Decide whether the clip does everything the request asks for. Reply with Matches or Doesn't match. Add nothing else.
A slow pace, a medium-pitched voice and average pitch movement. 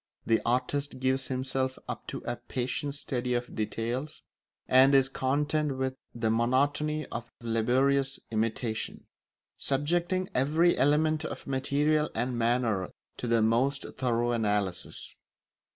Doesn't match